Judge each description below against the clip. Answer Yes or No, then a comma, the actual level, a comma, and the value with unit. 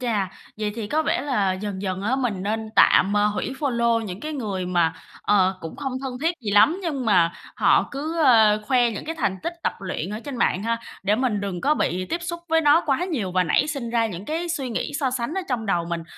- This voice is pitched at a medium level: No, high, 225 Hz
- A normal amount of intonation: No, wide, 6.1 semitones